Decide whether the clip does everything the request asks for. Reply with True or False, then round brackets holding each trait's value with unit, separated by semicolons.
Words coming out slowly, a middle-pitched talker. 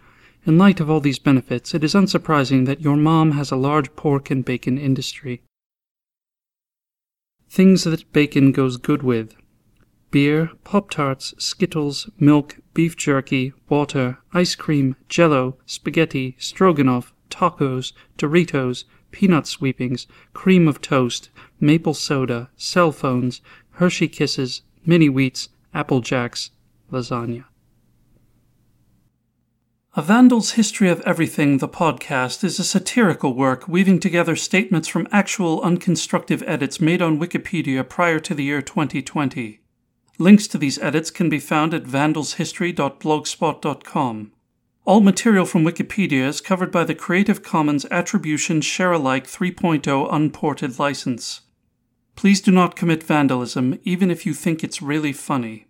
True (125 wpm; 150 Hz)